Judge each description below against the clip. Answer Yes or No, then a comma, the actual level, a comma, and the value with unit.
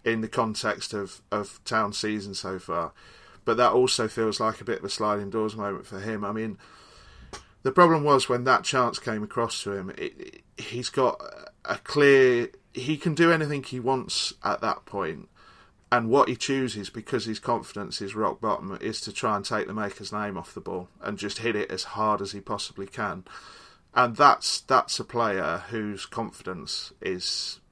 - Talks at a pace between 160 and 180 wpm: No, average, 195 wpm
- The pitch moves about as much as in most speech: Yes, average, 4.1 semitones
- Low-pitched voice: Yes, low, 110 Hz